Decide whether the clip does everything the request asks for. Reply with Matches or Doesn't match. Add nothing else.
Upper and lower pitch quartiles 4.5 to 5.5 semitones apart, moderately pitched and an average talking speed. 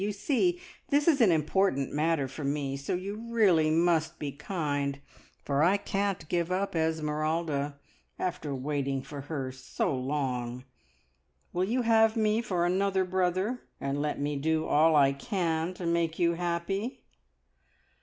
Matches